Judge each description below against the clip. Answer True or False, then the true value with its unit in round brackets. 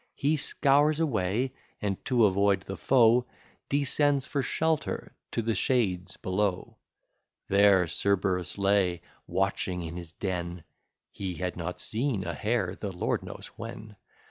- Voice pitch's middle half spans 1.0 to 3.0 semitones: False (5.3 semitones)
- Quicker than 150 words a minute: False (135 wpm)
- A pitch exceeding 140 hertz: False (100 Hz)